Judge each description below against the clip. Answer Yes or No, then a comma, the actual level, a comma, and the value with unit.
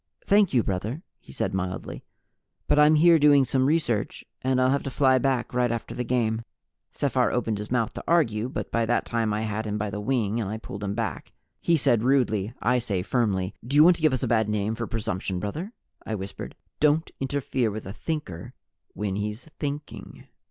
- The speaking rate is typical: No, fast, 210 wpm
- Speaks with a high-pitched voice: No, low, 115 Hz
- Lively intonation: No, average, 4.5 semitones